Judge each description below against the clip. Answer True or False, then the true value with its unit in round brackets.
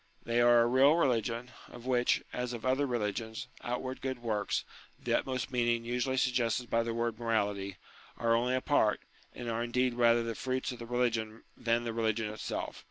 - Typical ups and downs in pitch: False (1.4 semitones)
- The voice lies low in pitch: True (120 Hz)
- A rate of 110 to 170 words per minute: False (185 wpm)